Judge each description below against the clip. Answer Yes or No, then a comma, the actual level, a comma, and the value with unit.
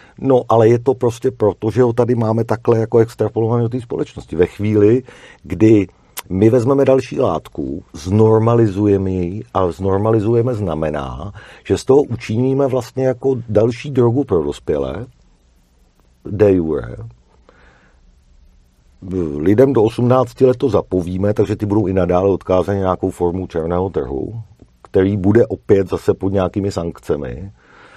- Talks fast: No, average, 135 wpm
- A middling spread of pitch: Yes, average, 4.5 semitones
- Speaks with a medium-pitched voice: No, low, 105 Hz